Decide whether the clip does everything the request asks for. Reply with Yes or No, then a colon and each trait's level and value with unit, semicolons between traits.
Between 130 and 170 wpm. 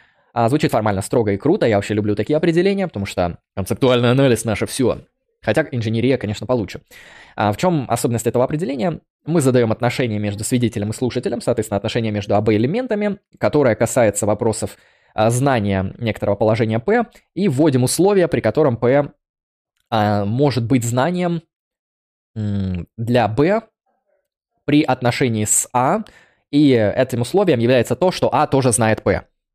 Yes: average, 140 wpm